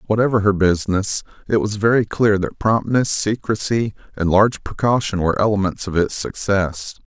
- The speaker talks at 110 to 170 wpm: Yes, average, 155 wpm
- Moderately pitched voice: No, low, 100 Hz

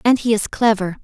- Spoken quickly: Yes, fast, 230 wpm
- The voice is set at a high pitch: Yes, high, 215 Hz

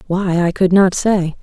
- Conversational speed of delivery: No, fast, 210 wpm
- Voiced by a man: No, female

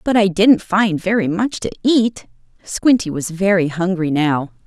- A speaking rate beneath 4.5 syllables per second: Yes, 4.3 syllables/s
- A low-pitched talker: No, high, 190 Hz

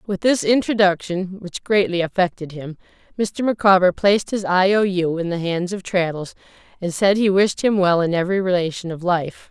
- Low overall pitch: No, medium, 185 Hz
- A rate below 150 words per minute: No, average, 190 wpm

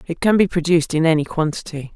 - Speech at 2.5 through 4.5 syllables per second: No, 6.6 syllables/s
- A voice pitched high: No, medium, 165 Hz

